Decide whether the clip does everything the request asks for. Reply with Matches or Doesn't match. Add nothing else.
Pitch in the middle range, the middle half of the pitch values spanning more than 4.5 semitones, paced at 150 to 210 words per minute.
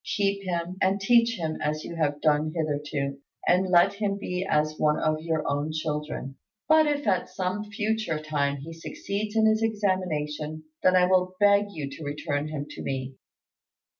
Matches